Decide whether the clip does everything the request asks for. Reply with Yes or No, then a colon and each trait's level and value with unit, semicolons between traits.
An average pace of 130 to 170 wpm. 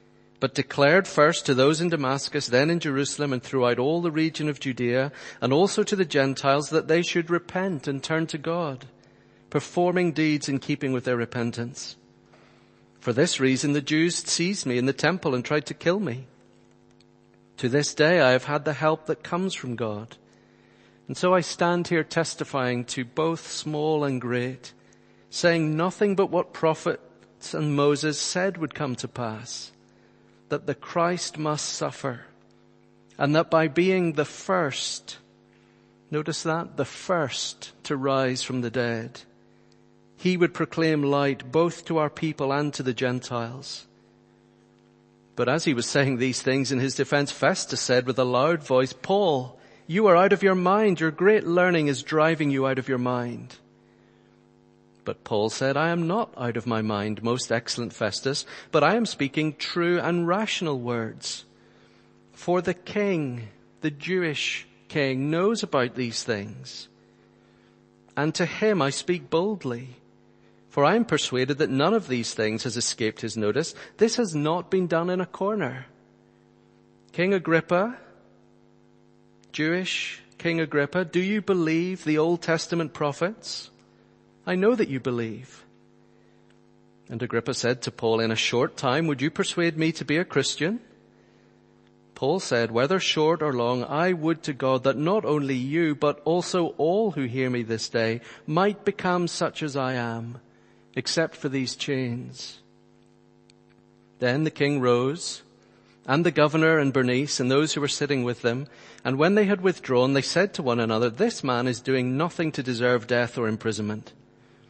Yes: average, 165 wpm